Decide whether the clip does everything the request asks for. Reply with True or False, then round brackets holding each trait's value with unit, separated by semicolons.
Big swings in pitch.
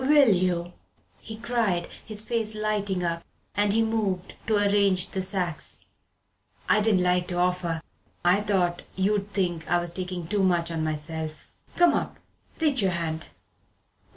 False (3.3 semitones)